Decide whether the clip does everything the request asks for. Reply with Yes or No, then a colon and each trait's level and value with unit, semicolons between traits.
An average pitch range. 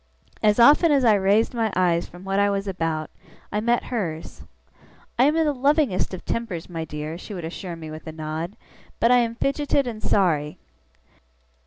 No: wide, 6.3 semitones